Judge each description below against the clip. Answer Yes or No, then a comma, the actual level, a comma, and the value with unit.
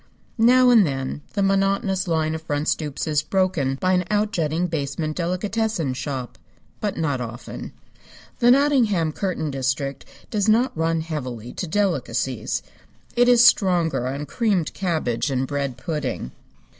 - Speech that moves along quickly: No, average, 140 wpm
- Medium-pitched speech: Yes, medium, 165 Hz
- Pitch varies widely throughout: Yes, wide, 5.8 semitones